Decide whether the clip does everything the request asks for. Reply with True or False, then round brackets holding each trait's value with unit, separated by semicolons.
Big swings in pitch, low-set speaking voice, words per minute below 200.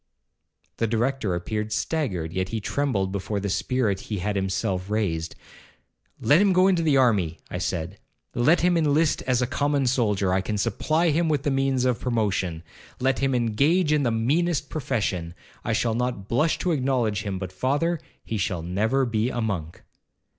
True (6.2 semitones; 115 Hz; 175 wpm)